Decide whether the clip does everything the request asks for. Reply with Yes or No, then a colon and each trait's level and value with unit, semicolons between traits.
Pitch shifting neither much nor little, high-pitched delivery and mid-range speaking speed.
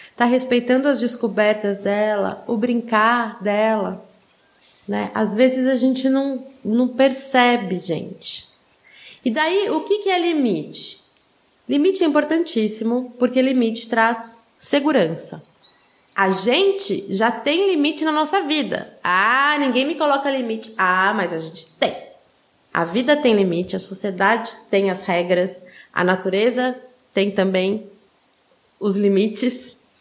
Yes: average, 4.9 semitones; high, 235 Hz; average, 130 wpm